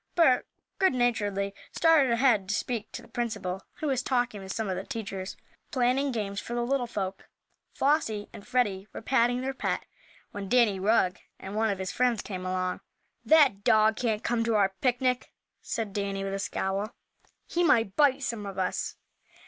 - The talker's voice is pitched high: Yes, high, 225 Hz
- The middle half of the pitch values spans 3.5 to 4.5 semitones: Yes, average, 4.2 semitones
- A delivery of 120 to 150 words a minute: No, average, 180 wpm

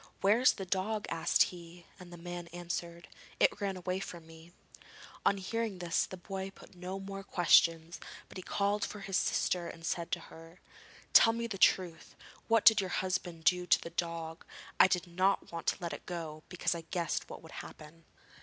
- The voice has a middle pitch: Yes, medium, 180 Hz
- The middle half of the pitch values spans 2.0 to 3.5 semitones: Yes, narrow, 2.4 semitones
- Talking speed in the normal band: Yes, average, 190 wpm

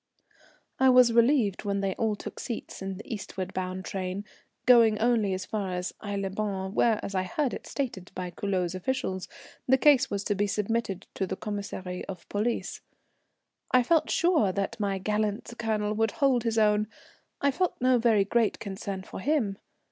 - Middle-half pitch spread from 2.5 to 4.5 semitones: Yes, average, 3.5 semitones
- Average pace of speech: Yes, average, 185 wpm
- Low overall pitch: No, high, 210 Hz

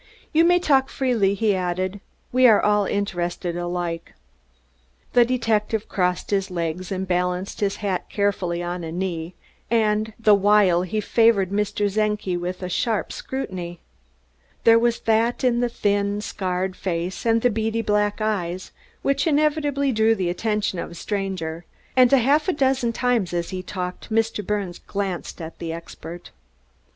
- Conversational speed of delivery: Yes, average, 155 wpm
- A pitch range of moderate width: Yes, average, 4.0 semitones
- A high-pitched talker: Yes, high, 205 Hz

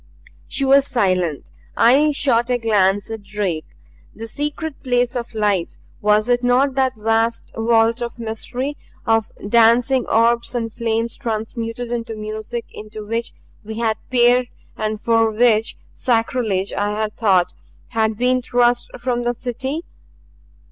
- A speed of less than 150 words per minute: Yes, average, 140 wpm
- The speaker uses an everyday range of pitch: No, narrow, 2.2 semitones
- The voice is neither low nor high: No, high, 230 Hz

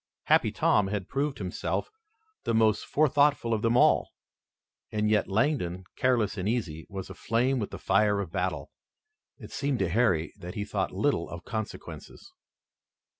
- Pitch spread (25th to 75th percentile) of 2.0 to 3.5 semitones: No, average, 4.3 semitones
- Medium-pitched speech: No, low, 105 Hz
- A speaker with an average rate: Yes, average, 155 wpm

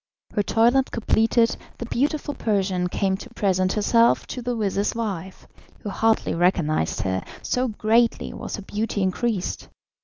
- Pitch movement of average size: Yes, average, 3.7 semitones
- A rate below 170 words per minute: Yes, average, 145 wpm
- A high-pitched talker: Yes, high, 210 Hz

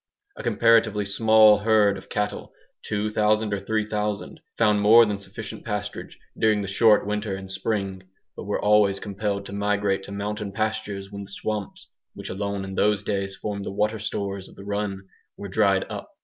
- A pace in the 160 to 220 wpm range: Yes, average, 175 wpm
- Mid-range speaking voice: No, low, 105 Hz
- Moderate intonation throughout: No, narrow, 1.3 semitones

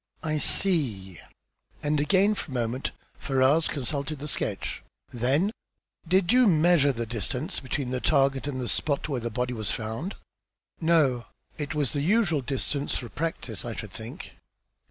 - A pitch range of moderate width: Yes, average, 4.4 semitones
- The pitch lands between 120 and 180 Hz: Yes, medium, 140 Hz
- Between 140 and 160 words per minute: Yes, average, 155 wpm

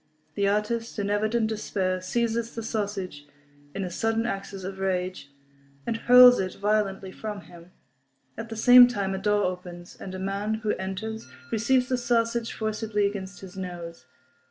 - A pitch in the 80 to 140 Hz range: No, high, 205 Hz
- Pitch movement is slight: No, average, 3.0 semitones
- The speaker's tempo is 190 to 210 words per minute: No, average, 160 wpm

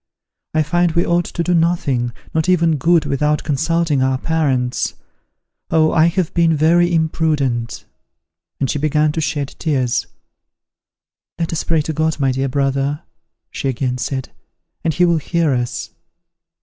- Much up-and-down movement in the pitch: No, average, 3.4 semitones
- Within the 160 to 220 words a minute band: No, average, 150 wpm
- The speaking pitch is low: No, medium, 155 Hz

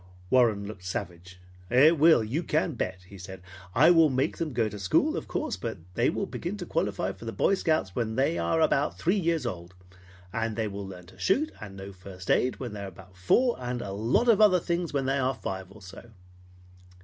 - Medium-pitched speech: No, low, 115 Hz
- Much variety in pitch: Yes, wide, 8.1 semitones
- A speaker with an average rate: No, fast, 220 wpm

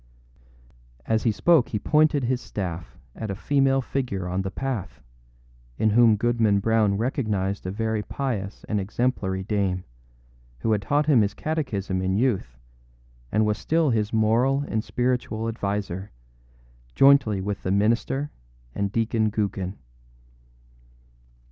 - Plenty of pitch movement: No, average, 4.0 semitones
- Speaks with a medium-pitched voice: No, low, 110 Hz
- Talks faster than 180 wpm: No, slow, 135 wpm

